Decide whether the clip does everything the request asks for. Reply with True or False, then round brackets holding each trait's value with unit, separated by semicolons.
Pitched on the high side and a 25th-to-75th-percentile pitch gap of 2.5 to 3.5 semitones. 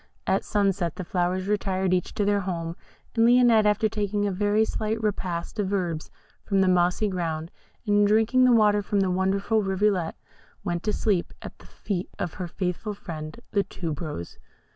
True (195 Hz; 2.8 semitones)